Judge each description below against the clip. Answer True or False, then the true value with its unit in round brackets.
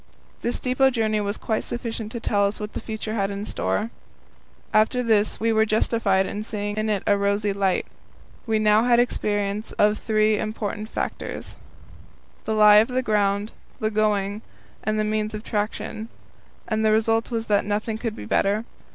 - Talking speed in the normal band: True (180 wpm)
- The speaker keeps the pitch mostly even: True (1.3 semitones)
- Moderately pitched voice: False (215 Hz)